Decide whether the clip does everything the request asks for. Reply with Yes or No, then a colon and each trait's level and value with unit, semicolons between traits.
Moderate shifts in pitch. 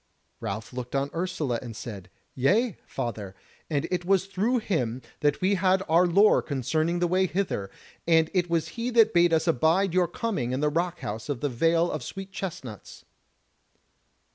No: wide, 6.1 semitones